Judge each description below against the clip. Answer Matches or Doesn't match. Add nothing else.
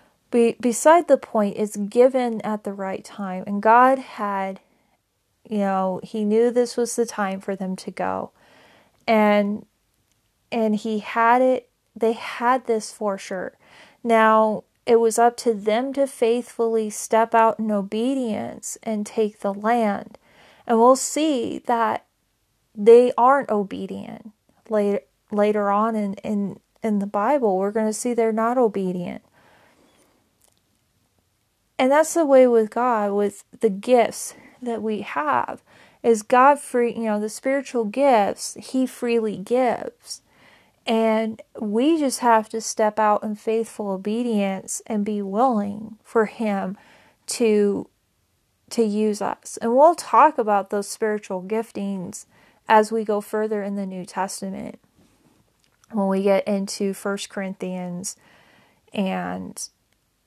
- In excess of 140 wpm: Doesn't match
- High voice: Matches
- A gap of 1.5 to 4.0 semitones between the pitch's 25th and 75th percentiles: Matches